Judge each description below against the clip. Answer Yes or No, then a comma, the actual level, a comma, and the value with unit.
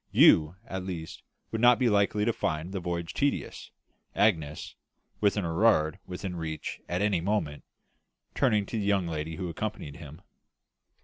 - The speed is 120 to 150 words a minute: No, average, 160 wpm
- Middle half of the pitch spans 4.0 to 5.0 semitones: Yes, average, 4.4 semitones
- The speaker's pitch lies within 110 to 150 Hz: No, very low, 90 Hz